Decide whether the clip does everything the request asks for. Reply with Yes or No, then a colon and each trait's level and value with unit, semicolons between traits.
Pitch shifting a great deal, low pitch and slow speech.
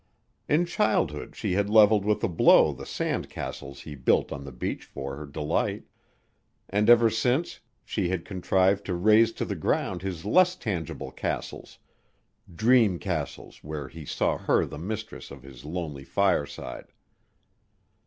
No: wide, 6.4 semitones; very low, 95 Hz; average, 155 wpm